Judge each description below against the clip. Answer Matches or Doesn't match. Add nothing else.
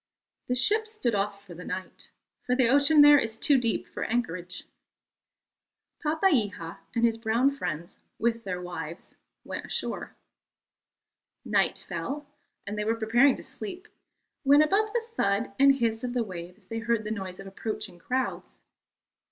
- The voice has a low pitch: Doesn't match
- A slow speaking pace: Doesn't match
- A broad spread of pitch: Matches